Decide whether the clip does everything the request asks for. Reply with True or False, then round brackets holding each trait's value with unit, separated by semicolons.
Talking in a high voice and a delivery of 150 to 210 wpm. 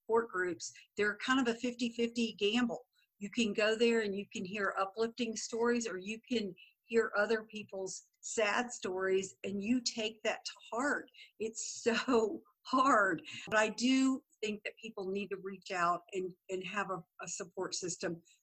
True (215 Hz; 170 wpm)